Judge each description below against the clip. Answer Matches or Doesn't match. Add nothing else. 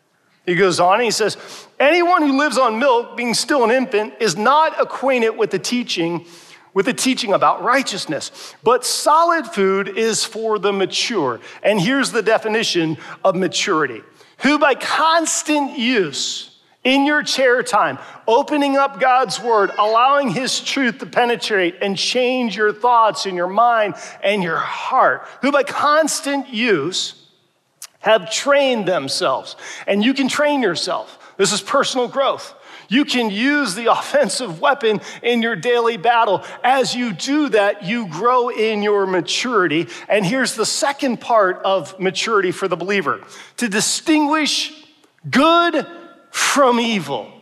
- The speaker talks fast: Doesn't match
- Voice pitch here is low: Doesn't match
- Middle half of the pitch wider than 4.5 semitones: Matches